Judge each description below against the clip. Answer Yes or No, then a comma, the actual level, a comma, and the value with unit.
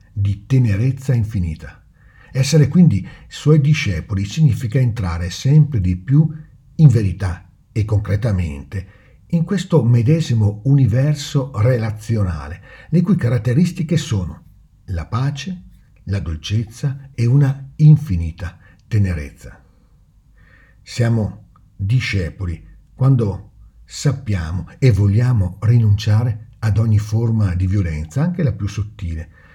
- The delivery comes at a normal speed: No, slow, 100 wpm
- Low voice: Yes, low, 110 Hz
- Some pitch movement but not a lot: No, wide, 6.0 semitones